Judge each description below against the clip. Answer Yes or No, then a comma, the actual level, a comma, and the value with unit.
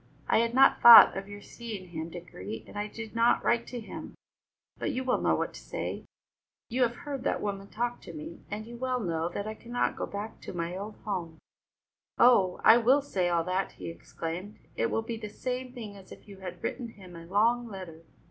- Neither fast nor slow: No, fast, 215 wpm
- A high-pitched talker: Yes, high, 210 Hz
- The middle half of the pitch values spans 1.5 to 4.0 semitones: No, average, 4.5 semitones